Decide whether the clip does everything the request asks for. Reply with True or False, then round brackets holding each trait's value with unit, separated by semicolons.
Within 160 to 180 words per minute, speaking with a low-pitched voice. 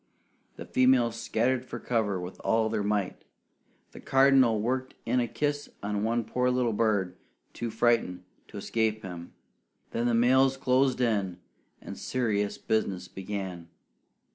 False (140 wpm; 115 Hz)